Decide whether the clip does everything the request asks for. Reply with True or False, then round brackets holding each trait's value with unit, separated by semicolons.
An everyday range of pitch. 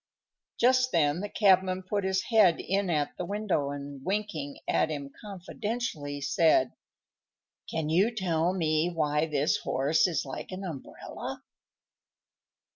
True (5.0 semitones)